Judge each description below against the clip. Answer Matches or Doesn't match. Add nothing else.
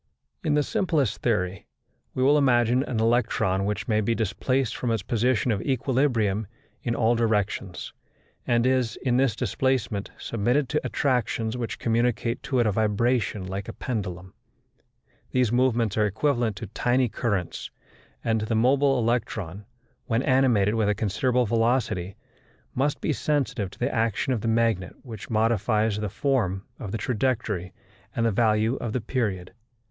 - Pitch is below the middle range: Matches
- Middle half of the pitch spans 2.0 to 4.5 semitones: Matches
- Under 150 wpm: Doesn't match